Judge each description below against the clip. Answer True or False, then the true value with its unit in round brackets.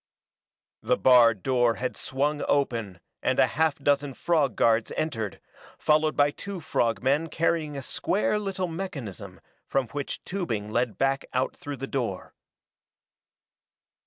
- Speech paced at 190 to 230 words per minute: False (135 wpm)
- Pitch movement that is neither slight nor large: True (4.7 semitones)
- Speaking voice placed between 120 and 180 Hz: True (135 Hz)